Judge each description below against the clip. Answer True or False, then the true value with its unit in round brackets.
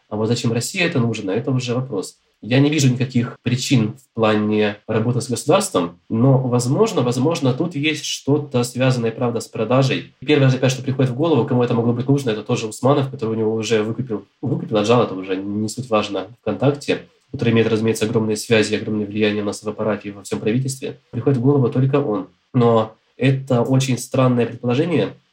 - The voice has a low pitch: True (120 Hz)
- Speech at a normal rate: False (190 wpm)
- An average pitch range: True (3.4 semitones)